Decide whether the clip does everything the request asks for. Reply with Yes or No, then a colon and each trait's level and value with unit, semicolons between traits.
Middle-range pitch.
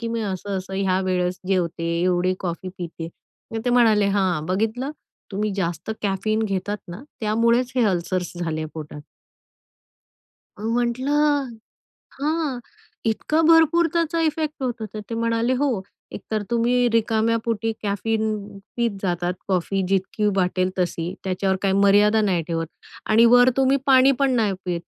No: high, 215 Hz